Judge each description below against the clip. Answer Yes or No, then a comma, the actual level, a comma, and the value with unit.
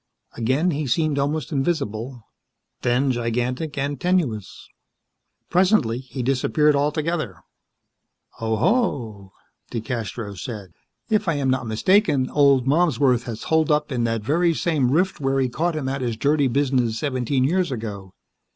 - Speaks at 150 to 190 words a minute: No, slow, 135 wpm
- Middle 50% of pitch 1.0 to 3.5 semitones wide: No, average, 4.5 semitones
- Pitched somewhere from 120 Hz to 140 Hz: Yes, low, 135 Hz